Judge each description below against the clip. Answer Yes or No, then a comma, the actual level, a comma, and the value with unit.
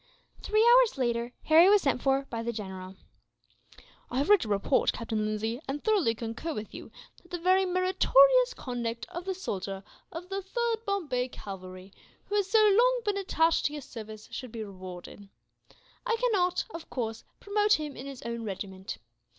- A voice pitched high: Yes, very high, 275 Hz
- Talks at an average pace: Yes, average, 175 wpm